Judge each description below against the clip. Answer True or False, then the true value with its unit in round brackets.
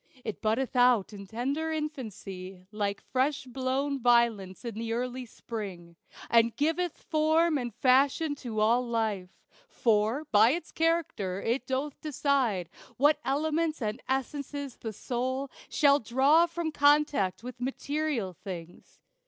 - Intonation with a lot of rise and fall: False (4.9 semitones)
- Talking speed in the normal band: False (130 wpm)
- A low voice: False (255 Hz)